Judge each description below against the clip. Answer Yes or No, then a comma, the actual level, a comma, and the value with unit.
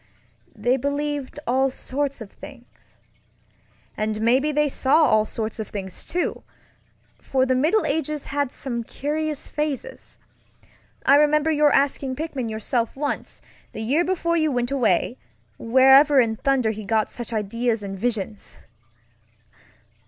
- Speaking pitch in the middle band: No, very high, 265 Hz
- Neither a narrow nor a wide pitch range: Yes, average, 4.6 semitones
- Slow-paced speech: Yes, slow, 130 wpm